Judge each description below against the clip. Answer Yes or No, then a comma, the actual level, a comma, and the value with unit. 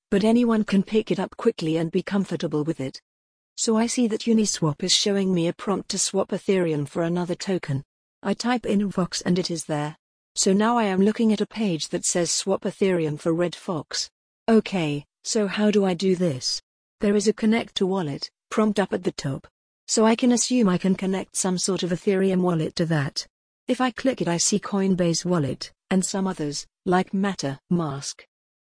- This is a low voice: No, high, 190 Hz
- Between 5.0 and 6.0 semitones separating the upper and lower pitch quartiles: No, average, 3.9 semitones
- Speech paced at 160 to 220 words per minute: Yes, average, 200 wpm